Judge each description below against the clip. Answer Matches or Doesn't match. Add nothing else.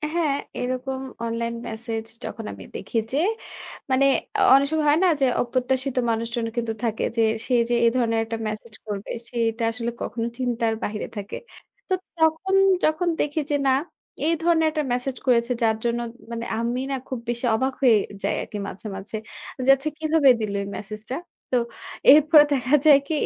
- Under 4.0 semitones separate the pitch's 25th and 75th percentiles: Matches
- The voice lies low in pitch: Doesn't match